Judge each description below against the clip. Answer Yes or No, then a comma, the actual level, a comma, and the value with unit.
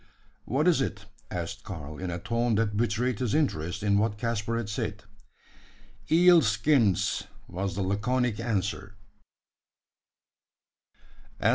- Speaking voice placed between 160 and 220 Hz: No, low, 105 Hz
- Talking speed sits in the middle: No, slow, 120 wpm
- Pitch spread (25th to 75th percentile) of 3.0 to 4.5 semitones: Yes, average, 3.4 semitones